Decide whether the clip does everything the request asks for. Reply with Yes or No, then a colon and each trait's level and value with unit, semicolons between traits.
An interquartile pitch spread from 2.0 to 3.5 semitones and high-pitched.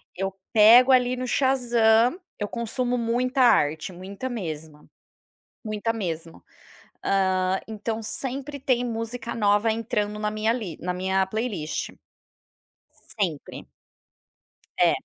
No: average, 4.3 semitones; high, 220 Hz